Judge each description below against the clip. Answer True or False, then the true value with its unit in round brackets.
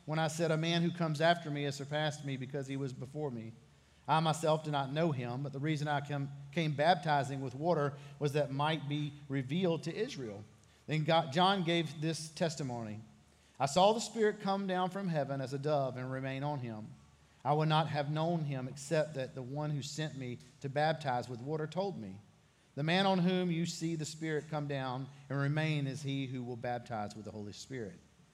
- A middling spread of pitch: True (3.3 semitones)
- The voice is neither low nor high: True (145 Hz)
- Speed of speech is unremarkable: False (210 wpm)